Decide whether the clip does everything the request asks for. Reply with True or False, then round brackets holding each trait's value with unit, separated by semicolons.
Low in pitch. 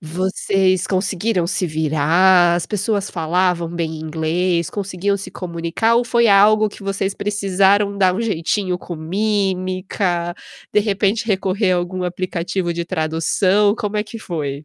False (185 Hz)